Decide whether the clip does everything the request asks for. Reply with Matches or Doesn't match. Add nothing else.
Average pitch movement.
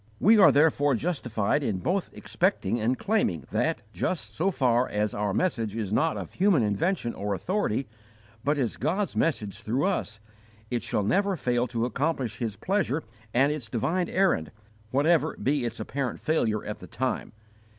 Doesn't match